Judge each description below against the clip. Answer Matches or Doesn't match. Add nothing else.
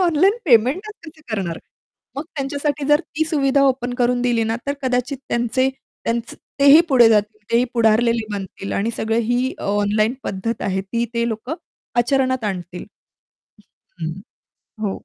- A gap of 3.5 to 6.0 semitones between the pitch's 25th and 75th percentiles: Matches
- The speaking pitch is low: Doesn't match